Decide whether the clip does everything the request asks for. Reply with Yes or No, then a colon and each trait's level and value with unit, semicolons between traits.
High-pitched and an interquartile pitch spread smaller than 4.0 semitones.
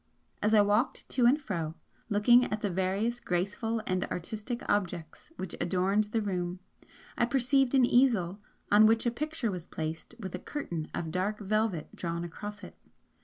No: high, 205 Hz; average, 4.5 semitones